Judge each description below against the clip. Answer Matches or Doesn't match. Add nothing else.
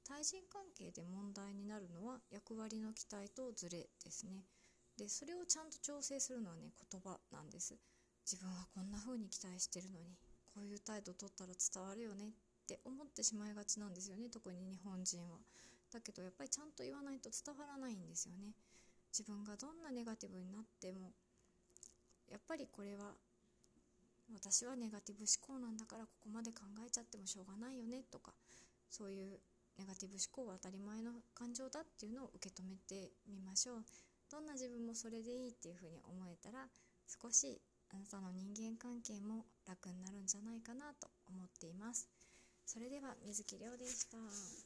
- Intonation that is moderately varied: Matches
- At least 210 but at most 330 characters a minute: Doesn't match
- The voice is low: Doesn't match